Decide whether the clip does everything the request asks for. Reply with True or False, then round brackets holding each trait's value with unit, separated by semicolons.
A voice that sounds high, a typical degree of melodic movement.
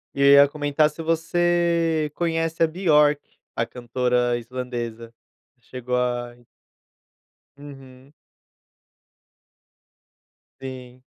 False (140 Hz; 4.4 semitones)